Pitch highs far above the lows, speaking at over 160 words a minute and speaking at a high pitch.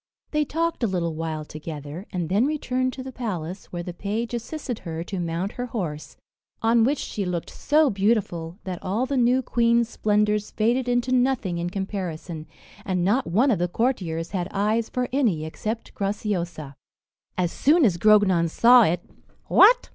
Yes: wide, 5.8 semitones; average, 170 wpm; high, 205 Hz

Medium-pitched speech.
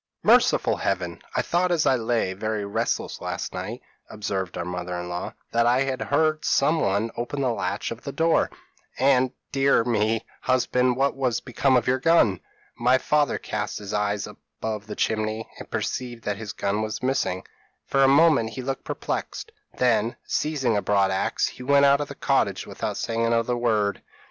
No: low, 115 Hz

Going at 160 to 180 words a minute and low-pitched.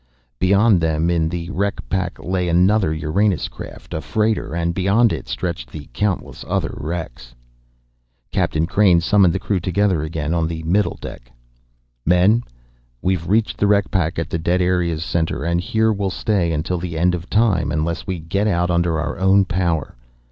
Yes: average, 175 wpm; very low, 90 Hz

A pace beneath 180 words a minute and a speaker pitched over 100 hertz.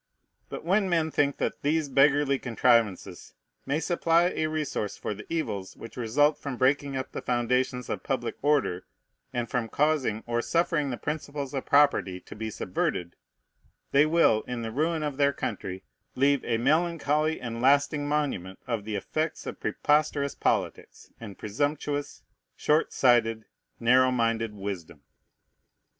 Yes: average, 150 wpm; low, 135 Hz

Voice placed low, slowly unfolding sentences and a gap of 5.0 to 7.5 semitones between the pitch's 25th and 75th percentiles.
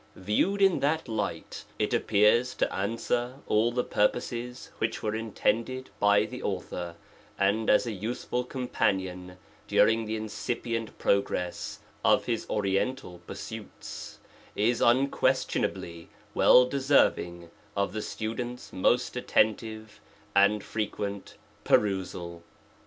No: low, 110 Hz; slow, 115 wpm; average, 3.6 semitones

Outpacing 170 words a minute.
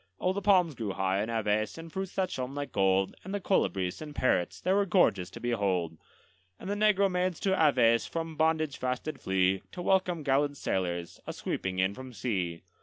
Yes: average, 200 wpm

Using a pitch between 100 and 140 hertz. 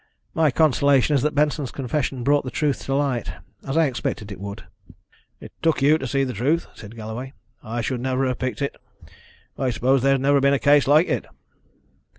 Yes: low, 135 Hz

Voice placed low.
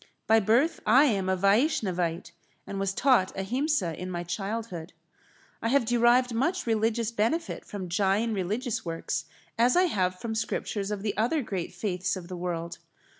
No: high, 210 Hz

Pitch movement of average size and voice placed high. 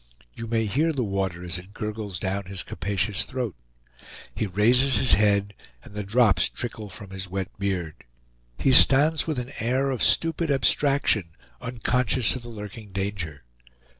No: average, 4.5 semitones; low, 105 Hz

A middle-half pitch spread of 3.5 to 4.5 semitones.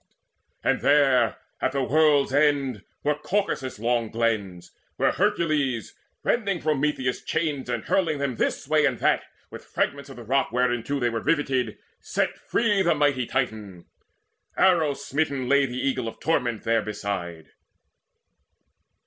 Yes: average, 4.1 semitones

